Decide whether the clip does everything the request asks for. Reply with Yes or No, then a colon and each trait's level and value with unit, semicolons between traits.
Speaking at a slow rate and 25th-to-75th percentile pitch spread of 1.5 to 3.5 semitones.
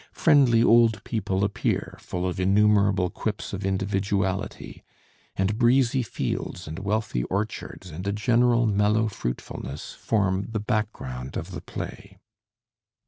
Yes: slow, 125 wpm; average, 2.9 semitones